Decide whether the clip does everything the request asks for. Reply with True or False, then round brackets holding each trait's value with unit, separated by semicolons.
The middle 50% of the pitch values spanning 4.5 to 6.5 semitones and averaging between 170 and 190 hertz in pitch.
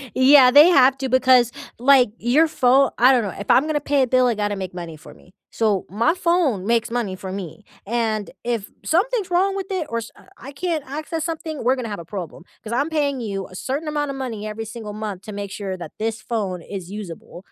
False (5.5 semitones; 240 Hz)